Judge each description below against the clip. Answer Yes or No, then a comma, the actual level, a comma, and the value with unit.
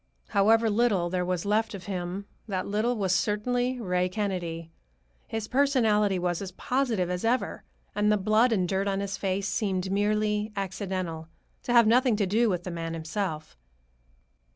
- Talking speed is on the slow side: No, average, 165 wpm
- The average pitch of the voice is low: No, high, 200 Hz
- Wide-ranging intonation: No, average, 3.3 semitones